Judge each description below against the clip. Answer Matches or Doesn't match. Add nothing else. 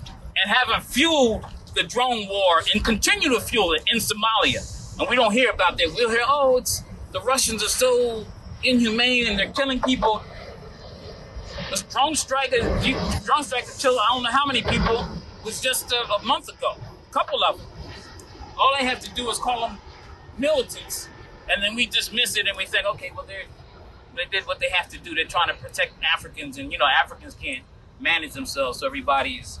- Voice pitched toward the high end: Matches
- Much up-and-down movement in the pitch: Doesn't match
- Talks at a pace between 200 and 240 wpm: Doesn't match